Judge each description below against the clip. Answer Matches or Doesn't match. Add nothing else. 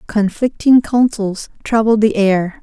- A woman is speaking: Matches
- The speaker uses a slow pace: Matches